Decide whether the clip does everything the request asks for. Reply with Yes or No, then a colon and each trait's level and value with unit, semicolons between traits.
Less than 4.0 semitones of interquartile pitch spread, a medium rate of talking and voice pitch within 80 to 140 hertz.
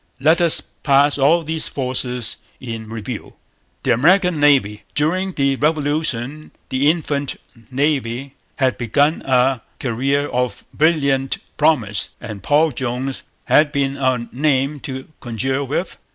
No: average, 3.1 semitones; slow, 125 wpm; low, 135 Hz